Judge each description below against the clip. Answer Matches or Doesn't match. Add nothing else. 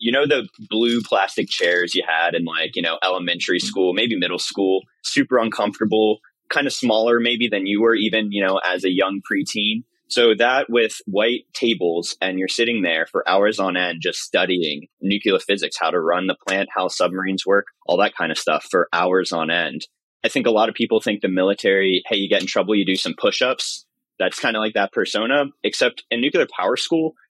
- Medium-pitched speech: Doesn't match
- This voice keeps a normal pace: Doesn't match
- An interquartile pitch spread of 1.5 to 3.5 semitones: Matches